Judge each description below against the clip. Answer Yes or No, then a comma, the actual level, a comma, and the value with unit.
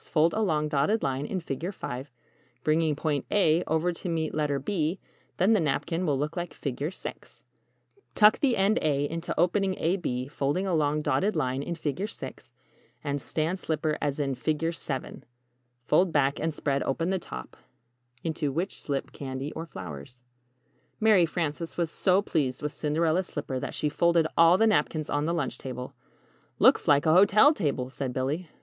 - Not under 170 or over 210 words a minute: Yes, average, 180 wpm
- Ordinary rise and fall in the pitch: Yes, average, 3.7 semitones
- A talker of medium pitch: Yes, medium, 155 Hz